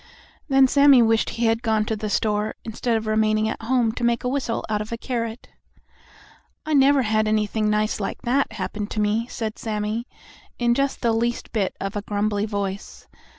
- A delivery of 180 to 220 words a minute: Yes, average, 195 wpm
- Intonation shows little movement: Yes, narrow, 2.0 semitones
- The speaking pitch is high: Yes, high, 220 Hz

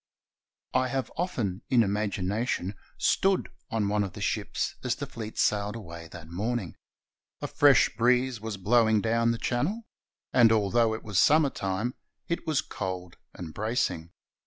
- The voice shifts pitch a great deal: No, average, 3.9 semitones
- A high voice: No, low, 110 Hz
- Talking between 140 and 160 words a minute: Yes, average, 155 wpm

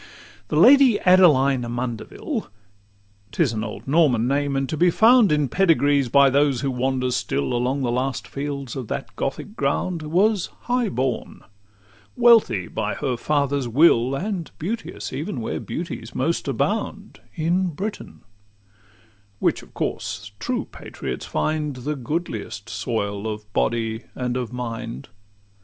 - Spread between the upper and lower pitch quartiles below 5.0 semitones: No, wide, 5.6 semitones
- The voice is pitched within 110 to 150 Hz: Yes, medium, 140 Hz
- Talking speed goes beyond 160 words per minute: No, average, 145 wpm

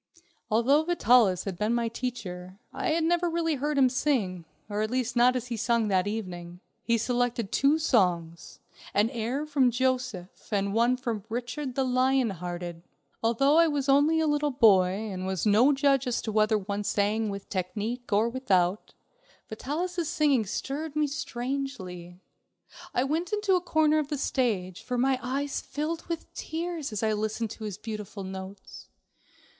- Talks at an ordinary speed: Yes, average, 170 wpm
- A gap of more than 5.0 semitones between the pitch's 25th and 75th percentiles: Yes, wide, 5.5 semitones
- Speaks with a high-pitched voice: Yes, high, 240 Hz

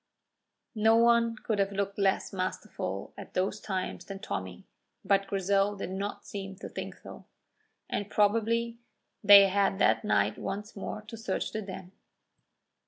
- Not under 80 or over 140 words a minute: No, average, 150 wpm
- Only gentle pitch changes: Yes, narrow, 1.8 semitones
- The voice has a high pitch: Yes, high, 200 Hz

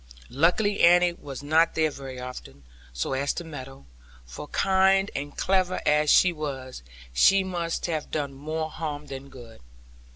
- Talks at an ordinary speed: Yes, average, 160 wpm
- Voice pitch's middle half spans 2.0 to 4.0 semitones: No, average, 4.4 semitones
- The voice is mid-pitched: Yes, medium, 150 Hz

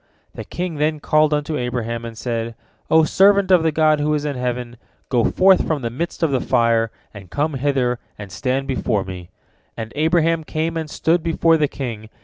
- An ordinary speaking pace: Yes, average, 195 wpm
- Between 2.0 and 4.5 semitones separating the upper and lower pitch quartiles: No, average, 5.2 semitones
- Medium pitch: Yes, medium, 145 Hz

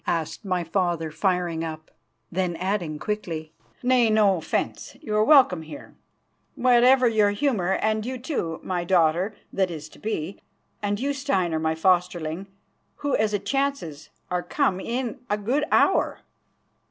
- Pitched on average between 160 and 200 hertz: Yes, high, 190 Hz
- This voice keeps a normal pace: Yes, average, 150 wpm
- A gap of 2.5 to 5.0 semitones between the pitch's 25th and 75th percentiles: No, wide, 5.5 semitones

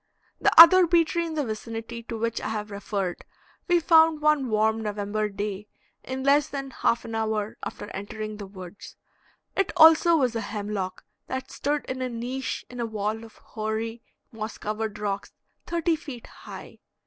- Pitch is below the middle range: No, high, 225 Hz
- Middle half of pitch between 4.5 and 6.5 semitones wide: Yes, average, 5.0 semitones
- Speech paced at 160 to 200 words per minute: Yes, average, 170 wpm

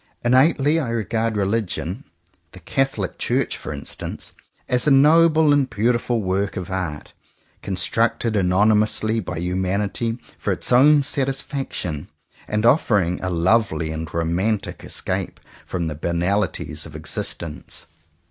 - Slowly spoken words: Yes, slow, 130 wpm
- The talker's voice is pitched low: Yes, low, 105 Hz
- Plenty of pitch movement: Yes, wide, 5.9 semitones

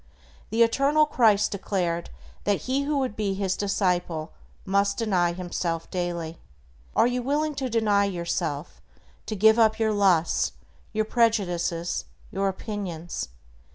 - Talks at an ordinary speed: No, slow, 130 wpm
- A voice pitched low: No, high, 200 Hz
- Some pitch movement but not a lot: Yes, average, 4.4 semitones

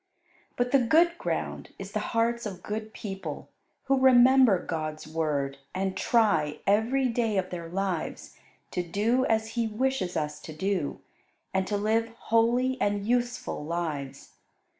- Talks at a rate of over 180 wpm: No, average, 145 wpm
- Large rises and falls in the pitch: Yes, wide, 5.8 semitones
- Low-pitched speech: No, high, 210 Hz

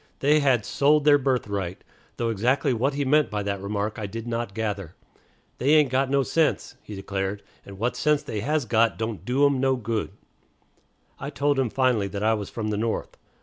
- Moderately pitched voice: No, low, 115 Hz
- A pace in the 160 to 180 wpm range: No, average, 200 wpm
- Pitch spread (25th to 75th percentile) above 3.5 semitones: Yes, average, 4.9 semitones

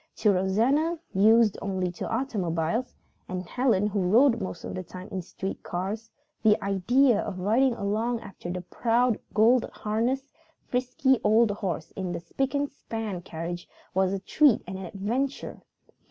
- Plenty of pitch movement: No, average, 4.7 semitones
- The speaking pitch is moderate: No, high, 210 Hz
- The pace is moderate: Yes, average, 155 wpm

